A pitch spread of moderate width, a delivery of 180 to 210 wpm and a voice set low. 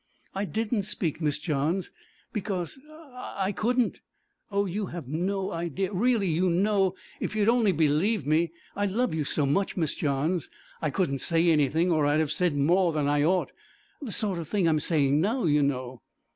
No: average, 4.8 semitones; average, 185 wpm; medium, 175 Hz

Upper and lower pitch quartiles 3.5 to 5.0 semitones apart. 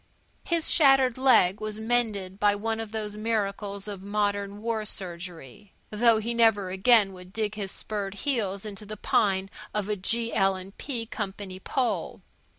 No: narrow, 2.5 semitones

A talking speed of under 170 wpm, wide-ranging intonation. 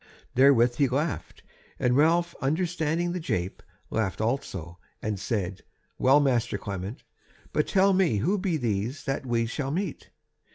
Yes: average, 140 wpm; wide, 6.7 semitones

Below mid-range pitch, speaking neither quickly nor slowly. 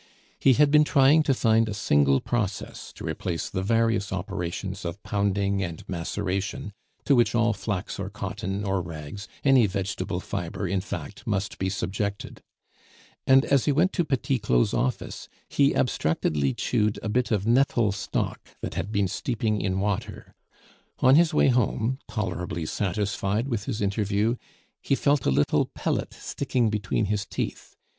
Yes: low, 105 Hz; average, 160 wpm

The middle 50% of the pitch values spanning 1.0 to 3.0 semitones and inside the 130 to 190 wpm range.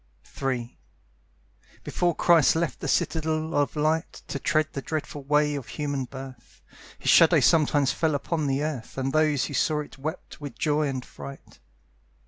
Yes: narrow, 2.4 semitones; average, 160 wpm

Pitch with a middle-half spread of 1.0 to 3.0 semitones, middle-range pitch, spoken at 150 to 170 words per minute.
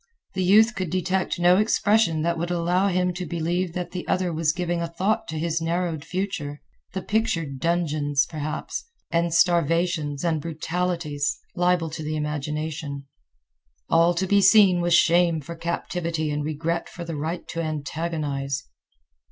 Yes: narrow, 2.5 semitones; medium, 170 Hz; average, 155 wpm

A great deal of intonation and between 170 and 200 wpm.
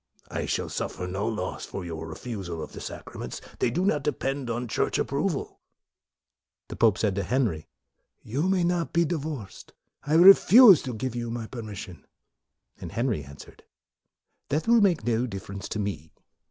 Yes: wide, 7.2 semitones; average, 175 wpm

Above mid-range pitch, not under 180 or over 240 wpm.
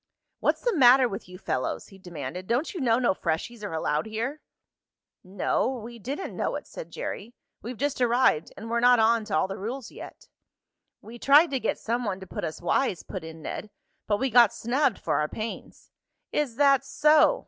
Yes: high, 230 Hz; average, 200 wpm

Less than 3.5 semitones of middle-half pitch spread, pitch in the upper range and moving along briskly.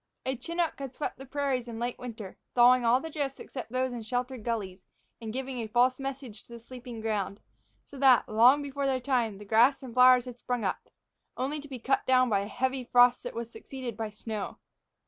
Yes: narrow, 2.6 semitones; very high, 250 Hz; fast, 220 wpm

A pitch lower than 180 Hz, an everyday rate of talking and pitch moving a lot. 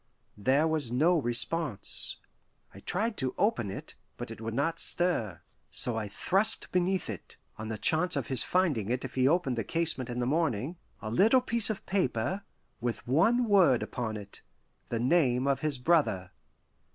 Yes: medium, 140 Hz; average, 175 wpm; wide, 7.0 semitones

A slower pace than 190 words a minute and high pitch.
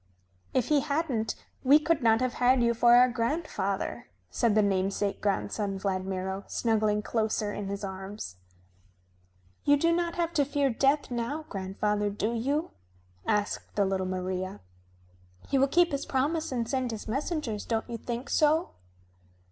Yes: average, 155 wpm; high, 230 Hz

